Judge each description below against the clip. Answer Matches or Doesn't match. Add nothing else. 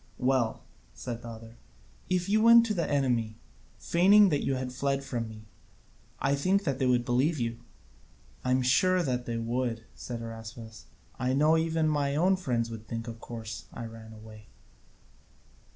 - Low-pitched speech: Matches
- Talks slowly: Doesn't match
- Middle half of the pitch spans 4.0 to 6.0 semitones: Matches